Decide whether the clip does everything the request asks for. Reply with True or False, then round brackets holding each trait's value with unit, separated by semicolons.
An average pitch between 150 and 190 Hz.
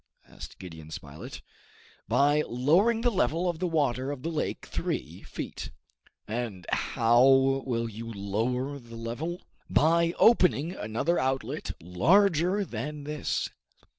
False (135 Hz)